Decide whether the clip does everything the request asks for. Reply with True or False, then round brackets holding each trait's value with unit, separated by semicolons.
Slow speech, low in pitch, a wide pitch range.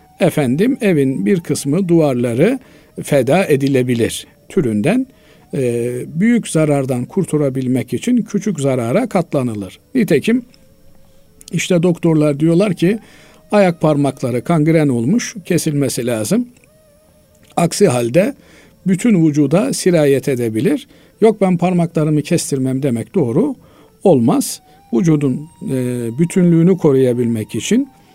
False (90 wpm; 155 Hz; 6.1 semitones)